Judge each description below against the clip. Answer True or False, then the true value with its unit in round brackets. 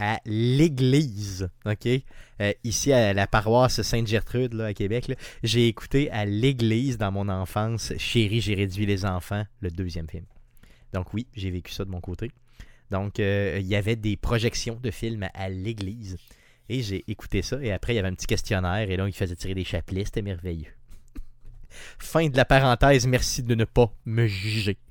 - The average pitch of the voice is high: False (105 Hz)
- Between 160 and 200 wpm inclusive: True (190 wpm)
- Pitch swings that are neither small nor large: True (3.7 semitones)